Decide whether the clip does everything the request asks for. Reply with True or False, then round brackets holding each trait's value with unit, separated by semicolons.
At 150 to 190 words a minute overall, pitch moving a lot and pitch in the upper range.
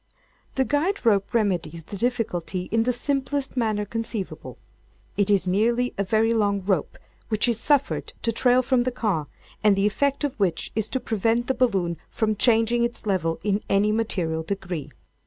False (175 wpm; 3.8 semitones; 220 Hz)